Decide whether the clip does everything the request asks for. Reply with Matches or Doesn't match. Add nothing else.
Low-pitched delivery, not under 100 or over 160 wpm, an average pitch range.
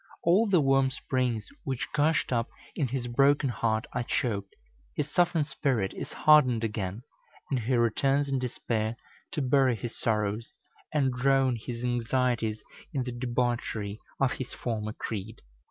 Matches